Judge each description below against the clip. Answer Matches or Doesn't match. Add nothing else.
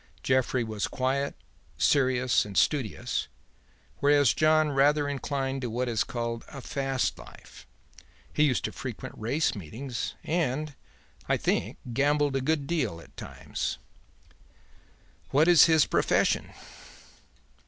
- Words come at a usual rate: Doesn't match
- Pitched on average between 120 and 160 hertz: Matches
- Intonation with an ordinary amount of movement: Matches